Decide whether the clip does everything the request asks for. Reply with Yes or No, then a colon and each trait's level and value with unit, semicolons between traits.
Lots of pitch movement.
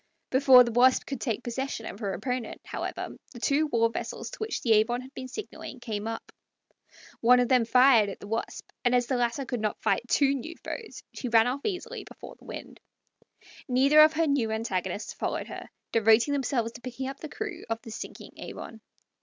No: average, 3.3 semitones